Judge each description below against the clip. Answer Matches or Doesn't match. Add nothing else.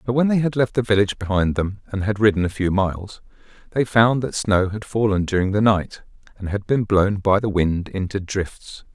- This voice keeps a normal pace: Doesn't match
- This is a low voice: Matches